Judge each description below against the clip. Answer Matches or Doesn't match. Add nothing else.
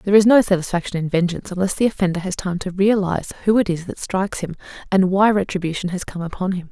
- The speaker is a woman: Matches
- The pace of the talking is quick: Matches